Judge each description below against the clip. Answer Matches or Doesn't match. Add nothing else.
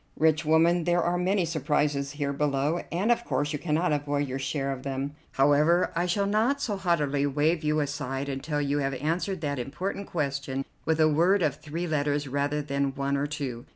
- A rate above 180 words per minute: Matches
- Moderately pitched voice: Matches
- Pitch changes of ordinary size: Matches